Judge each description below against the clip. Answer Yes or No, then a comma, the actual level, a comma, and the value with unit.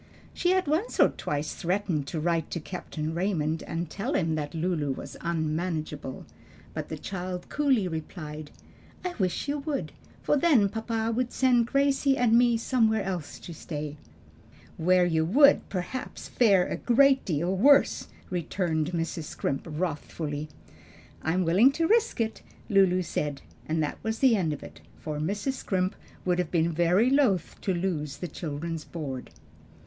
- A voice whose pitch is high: No, medium, 180 Hz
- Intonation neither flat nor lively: No, wide, 6.4 semitones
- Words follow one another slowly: No, average, 160 wpm